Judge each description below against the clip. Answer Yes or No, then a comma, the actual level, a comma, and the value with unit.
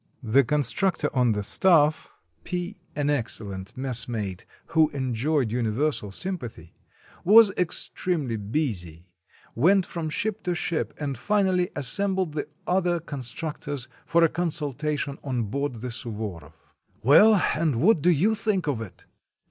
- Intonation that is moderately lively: No, wide, 6.9 semitones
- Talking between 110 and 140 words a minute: Yes, slow, 135 wpm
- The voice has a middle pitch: Yes, medium, 145 Hz